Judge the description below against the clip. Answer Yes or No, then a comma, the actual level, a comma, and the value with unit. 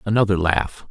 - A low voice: Yes, very low, 95 Hz